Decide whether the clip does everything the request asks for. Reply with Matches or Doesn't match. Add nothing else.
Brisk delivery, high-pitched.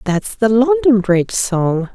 Doesn't match